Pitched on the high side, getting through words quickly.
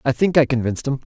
No: low, 130 Hz; fast, 270 wpm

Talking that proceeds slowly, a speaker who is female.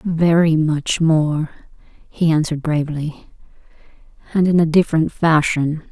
Yes: slow, 110 wpm; female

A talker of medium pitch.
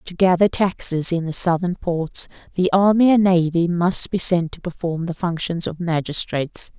Yes: medium, 175 Hz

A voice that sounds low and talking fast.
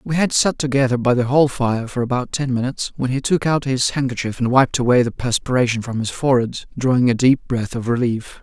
Yes: low, 125 Hz; fast, 230 wpm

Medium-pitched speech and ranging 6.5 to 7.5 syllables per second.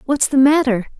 No: very high, 265 Hz; 6.7 syllables/s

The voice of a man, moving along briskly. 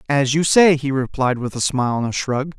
Yes: male; fast, 230 wpm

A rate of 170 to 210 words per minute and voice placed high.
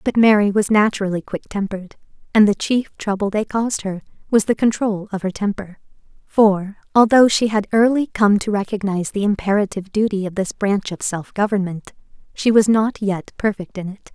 Yes: average, 180 wpm; high, 205 Hz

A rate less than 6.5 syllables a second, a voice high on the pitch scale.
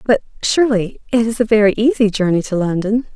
Yes: 5.9 syllables/s; high, 215 Hz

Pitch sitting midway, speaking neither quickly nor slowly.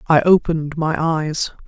Yes: medium, 160 Hz; average, 145 wpm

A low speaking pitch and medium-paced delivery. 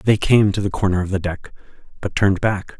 No: low, 100 Hz; fast, 235 wpm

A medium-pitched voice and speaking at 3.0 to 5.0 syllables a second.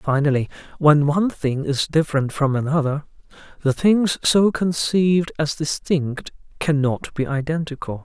Yes: medium, 150 Hz; 4.6 syllables/s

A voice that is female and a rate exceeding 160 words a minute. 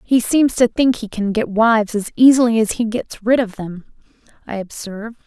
Yes: female; fast, 205 wpm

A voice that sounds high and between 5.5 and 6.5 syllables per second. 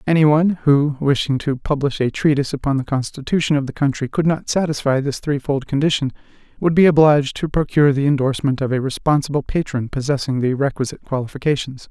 No: medium, 140 Hz; 6.3 syllables/s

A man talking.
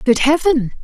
No: female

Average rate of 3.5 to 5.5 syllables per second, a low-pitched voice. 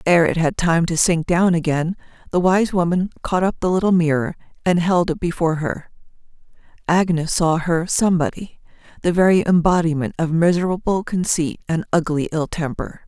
No: 5.3 syllables/s; medium, 170 Hz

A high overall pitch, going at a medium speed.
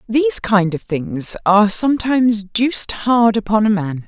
Yes: high, 215 Hz; average, 160 wpm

